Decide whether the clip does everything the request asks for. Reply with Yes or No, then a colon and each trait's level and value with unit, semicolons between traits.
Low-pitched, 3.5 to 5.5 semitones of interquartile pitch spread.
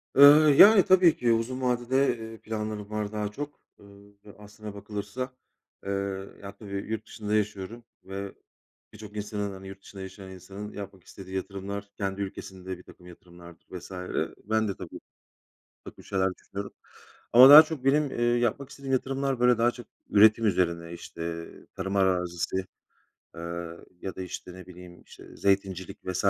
Yes: low, 100 Hz; average, 3.8 semitones